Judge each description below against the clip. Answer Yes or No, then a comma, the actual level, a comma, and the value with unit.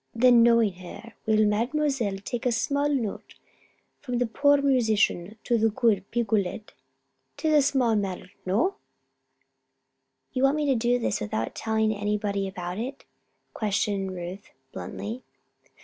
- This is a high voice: Yes, high, 225 Hz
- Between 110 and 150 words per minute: Yes, average, 140 wpm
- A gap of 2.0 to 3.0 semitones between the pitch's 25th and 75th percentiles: No, average, 3.9 semitones